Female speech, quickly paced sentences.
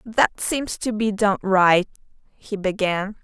No: female; average, 150 wpm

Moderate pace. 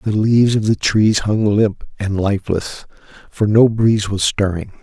Yes: average, 175 wpm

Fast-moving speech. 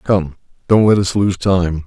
No: average, 195 wpm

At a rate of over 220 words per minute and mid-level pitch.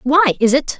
No: fast, 230 wpm; very high, 270 Hz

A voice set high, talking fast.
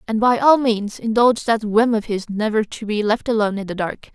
Yes: high, 220 Hz; fast, 245 wpm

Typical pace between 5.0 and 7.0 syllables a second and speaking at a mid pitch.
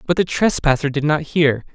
Yes: 5.2 syllables/s; medium, 155 Hz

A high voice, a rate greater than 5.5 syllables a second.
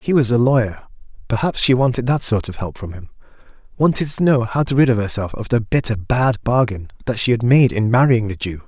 No: low, 120 Hz; 5.7 syllables/s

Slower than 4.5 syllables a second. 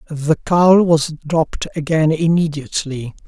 Yes: 4.3 syllables/s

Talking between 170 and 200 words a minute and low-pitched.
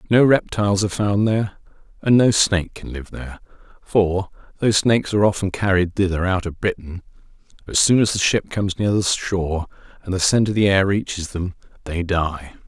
Yes: average, 190 wpm; very low, 95 Hz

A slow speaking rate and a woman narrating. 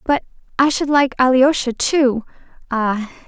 Yes: slow, 130 wpm; female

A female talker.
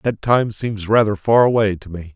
No: male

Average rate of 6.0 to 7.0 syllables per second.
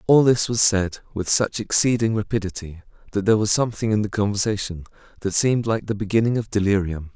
Yes: 6.1 syllables/s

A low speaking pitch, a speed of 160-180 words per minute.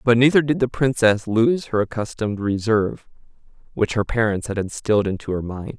Yes: low, 115 Hz; average, 175 wpm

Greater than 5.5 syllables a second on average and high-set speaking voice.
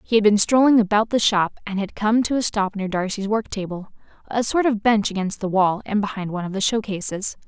Yes: 5.7 syllables/s; high, 205 Hz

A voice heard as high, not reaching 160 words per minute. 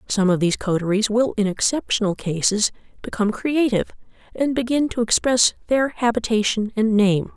Yes: high, 220 Hz; average, 145 wpm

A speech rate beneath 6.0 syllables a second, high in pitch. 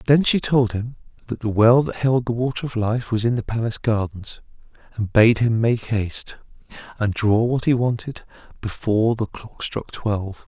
No: 4.9 syllables/s; low, 115 Hz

